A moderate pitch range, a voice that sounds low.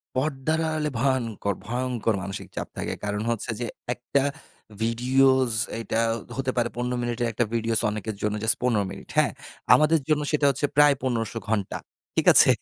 Yes: average, 3.1 semitones; low, 120 Hz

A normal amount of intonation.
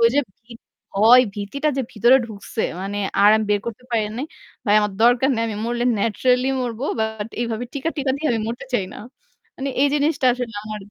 Yes: average, 3.3 semitones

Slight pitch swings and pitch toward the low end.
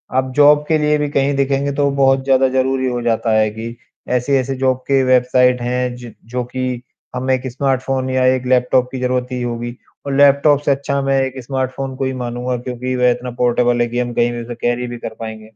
Yes: narrow, 1.7 semitones; low, 130 Hz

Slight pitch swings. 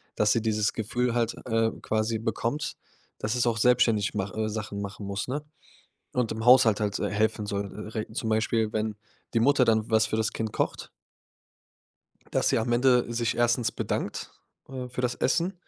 Yes: narrow, 2.2 semitones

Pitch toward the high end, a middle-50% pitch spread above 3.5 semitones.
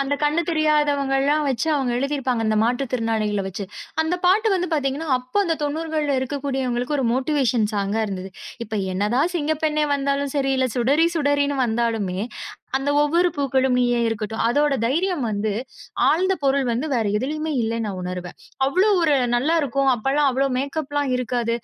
Yes: very high, 275 Hz; average, 3.9 semitones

